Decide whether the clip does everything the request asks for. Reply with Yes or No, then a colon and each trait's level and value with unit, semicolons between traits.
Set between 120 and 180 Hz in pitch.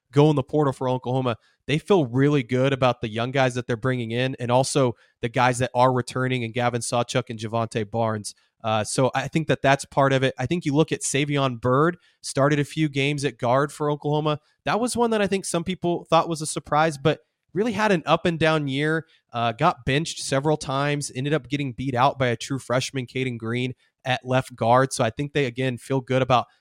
Yes: low, 135 Hz